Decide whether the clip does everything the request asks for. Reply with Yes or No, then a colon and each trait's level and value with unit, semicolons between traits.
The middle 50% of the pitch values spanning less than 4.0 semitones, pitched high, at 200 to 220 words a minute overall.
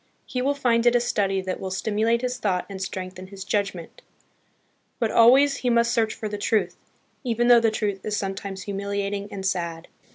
No: average, 3.5 semitones; high, 205 Hz; average, 190 wpm